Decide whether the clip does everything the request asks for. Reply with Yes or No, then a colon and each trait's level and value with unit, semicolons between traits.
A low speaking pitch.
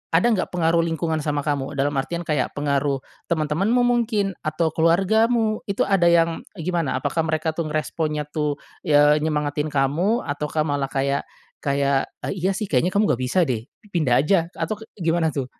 No: medium, 160 Hz